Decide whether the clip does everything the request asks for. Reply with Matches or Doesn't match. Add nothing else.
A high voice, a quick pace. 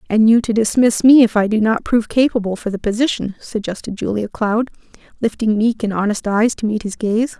Matches